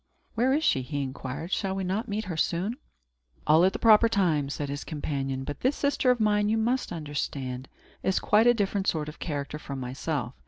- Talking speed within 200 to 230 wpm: Yes, fast, 205 wpm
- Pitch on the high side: No, medium, 170 Hz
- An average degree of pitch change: No, wide, 7.1 semitones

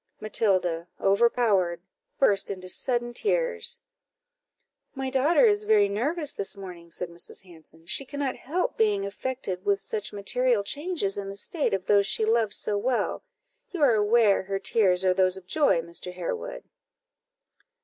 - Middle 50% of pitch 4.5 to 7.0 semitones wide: Yes, average, 5.2 semitones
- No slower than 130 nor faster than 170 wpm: Yes, average, 150 wpm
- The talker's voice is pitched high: Yes, high, 205 Hz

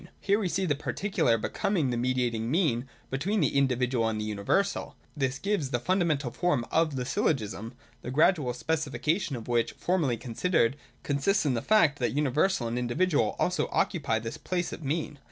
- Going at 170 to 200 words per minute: Yes, average, 175 wpm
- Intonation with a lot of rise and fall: Yes, wide, 6.1 semitones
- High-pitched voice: No, medium, 140 Hz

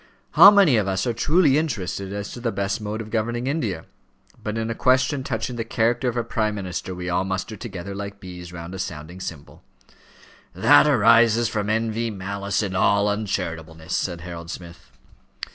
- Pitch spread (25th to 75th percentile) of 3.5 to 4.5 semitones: Yes, average, 4.0 semitones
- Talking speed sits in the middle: Yes, average, 180 wpm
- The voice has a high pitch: No, low, 105 Hz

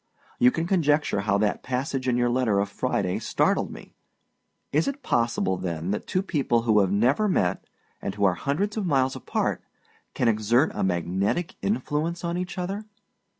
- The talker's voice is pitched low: Yes, low, 125 Hz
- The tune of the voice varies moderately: No, wide, 8.7 semitones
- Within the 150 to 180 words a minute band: Yes, average, 175 wpm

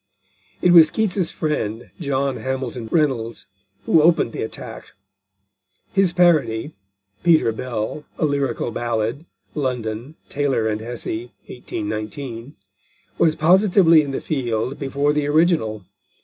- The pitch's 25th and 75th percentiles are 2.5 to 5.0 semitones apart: No, wide, 5.4 semitones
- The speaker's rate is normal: No, slow, 115 wpm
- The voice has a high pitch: No, low, 135 Hz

